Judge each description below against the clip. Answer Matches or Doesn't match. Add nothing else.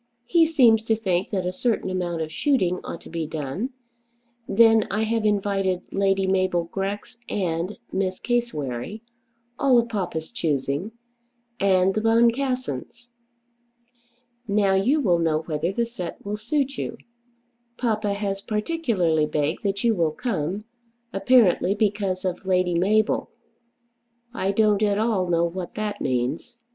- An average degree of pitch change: Matches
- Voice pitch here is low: Doesn't match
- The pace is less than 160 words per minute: Matches